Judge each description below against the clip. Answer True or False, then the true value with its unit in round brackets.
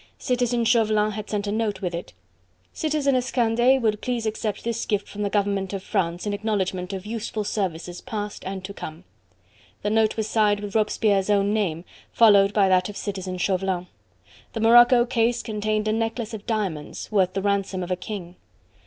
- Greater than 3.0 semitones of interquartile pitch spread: False (2.6 semitones)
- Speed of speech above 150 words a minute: True (180 wpm)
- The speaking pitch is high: True (210 Hz)